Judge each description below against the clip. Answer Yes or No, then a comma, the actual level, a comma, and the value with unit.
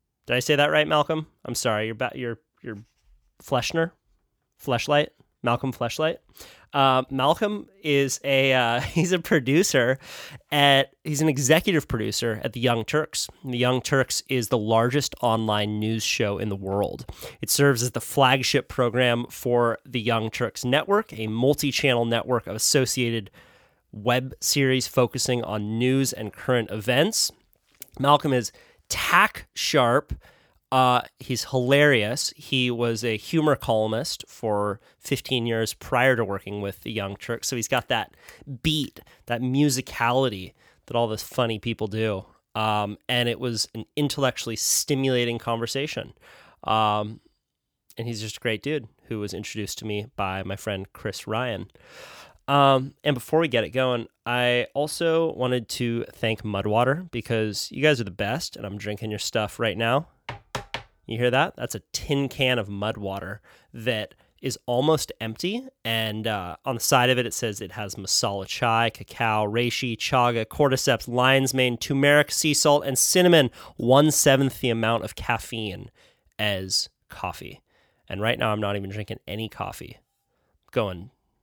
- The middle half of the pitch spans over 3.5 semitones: Yes, average, 3.9 semitones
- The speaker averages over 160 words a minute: No, average, 155 wpm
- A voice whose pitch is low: Yes, low, 120 Hz